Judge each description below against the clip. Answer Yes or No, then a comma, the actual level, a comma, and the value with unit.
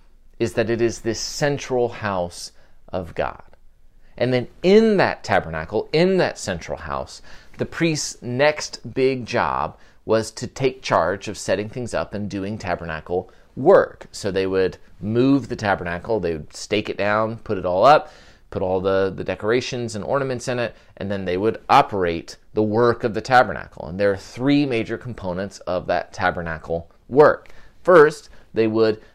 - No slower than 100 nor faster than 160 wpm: No, average, 170 wpm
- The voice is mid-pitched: No, low, 110 Hz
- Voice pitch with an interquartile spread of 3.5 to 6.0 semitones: Yes, average, 4.6 semitones